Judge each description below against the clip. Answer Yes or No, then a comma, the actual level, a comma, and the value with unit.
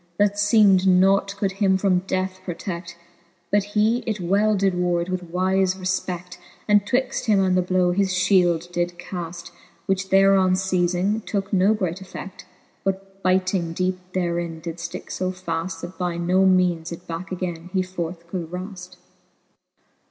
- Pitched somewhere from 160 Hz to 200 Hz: Yes, medium, 185 Hz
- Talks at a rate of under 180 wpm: Yes, average, 160 wpm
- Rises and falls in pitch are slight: Yes, narrow, 1.6 semitones